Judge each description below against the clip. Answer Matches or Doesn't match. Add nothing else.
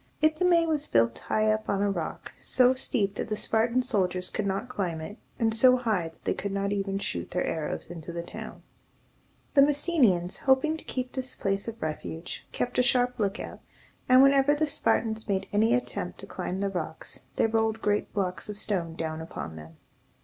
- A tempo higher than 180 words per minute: Matches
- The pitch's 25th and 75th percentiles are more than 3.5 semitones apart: Matches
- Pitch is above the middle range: Matches